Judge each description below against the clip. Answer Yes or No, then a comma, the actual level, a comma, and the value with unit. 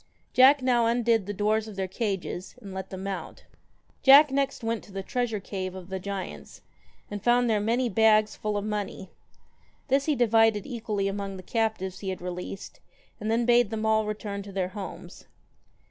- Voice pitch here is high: Yes, high, 210 Hz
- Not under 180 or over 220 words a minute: Yes, average, 190 wpm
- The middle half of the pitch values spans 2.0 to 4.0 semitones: Yes, average, 3.0 semitones